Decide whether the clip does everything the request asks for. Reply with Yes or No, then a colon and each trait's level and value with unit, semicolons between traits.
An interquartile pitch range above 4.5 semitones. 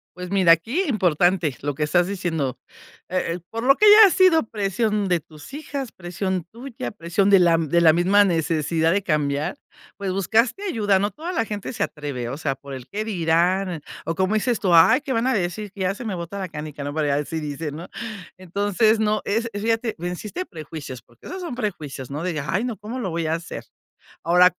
Yes: average, 5.0 semitones